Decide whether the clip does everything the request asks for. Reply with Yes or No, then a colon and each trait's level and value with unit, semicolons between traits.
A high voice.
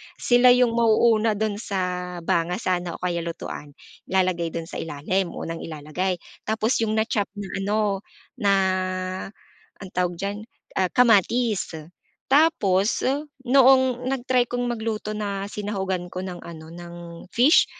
Yes: high, 200 Hz